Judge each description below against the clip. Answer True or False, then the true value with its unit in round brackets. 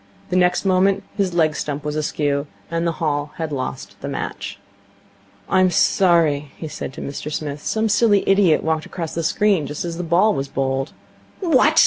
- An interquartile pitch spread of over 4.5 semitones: False (4.1 semitones)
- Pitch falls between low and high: True (165 Hz)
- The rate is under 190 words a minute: True (180 wpm)